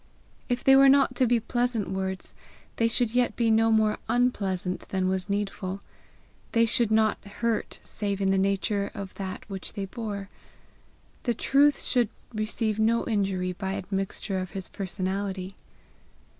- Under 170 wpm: Yes, average, 155 wpm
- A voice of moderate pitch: No, high, 205 Hz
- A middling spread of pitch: Yes, average, 3.2 semitones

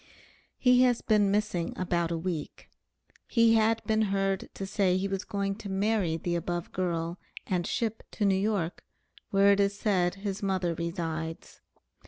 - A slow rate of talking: No, average, 165 wpm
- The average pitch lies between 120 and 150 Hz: No, high, 195 Hz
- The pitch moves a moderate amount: Yes, average, 3.1 semitones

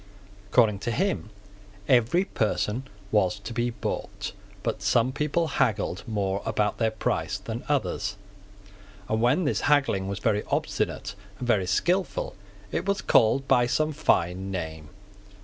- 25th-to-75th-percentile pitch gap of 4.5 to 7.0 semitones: Yes, wide, 5.4 semitones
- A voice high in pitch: No, low, 115 Hz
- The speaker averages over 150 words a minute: No, average, 140 wpm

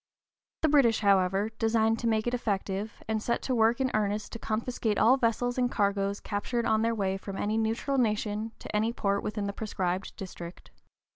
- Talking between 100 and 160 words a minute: No, average, 190 wpm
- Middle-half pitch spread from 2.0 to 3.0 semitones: Yes, narrow, 2.4 semitones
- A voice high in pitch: Yes, high, 220 Hz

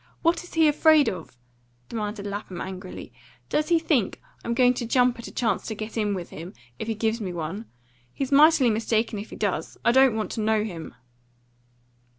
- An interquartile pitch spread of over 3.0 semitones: Yes, average, 4.3 semitones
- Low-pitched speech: No, high, 220 Hz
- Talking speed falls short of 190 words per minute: No, average, 195 wpm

